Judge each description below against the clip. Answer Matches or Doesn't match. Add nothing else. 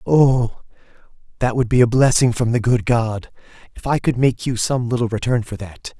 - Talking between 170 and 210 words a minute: Matches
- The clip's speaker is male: Matches